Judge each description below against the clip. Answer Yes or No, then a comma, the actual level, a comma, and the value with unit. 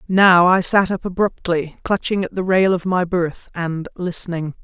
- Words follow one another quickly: No, average, 180 wpm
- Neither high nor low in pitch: Yes, medium, 180 Hz